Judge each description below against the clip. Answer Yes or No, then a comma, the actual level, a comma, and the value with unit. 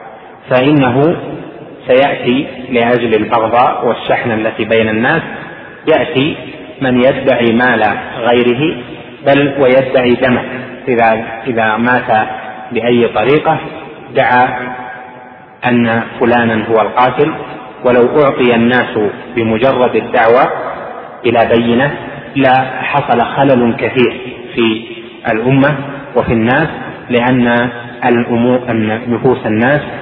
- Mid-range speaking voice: No, low, 125 Hz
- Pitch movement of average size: No, narrow, 2.0 semitones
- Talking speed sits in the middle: Yes, average, 85 wpm